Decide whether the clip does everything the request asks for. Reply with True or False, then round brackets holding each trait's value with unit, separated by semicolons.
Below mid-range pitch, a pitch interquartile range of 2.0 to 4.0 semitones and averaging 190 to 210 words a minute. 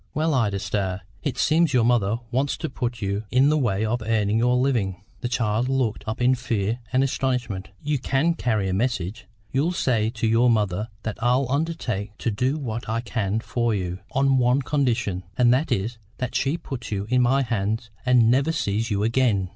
True (120 Hz; 3.5 semitones; 195 wpm)